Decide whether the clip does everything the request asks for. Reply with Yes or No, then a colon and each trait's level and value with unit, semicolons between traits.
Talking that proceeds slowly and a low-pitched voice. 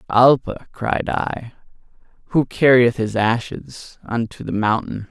Yes: slow, 120 wpm; low, 115 Hz